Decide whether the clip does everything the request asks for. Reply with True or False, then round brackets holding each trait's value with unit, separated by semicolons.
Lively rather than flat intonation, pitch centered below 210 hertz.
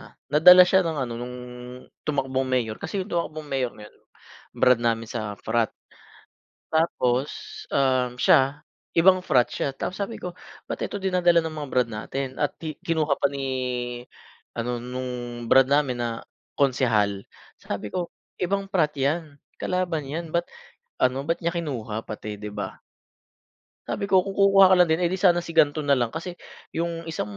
True (5.8 semitones; 140 Hz)